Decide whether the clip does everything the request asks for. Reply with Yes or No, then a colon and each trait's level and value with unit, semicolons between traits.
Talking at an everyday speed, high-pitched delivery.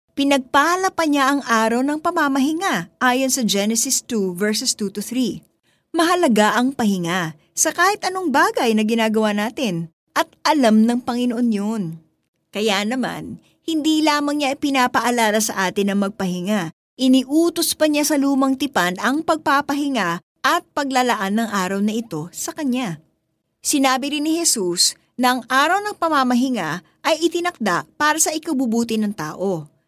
Yes: average, 145 wpm; very high, 250 Hz